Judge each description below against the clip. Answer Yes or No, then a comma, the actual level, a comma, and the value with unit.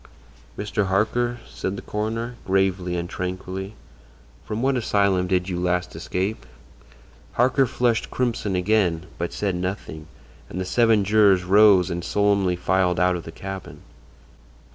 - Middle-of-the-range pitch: No, very low, 95 Hz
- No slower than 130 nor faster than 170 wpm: Yes, average, 140 wpm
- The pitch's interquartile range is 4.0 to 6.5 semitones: No, average, 2.9 semitones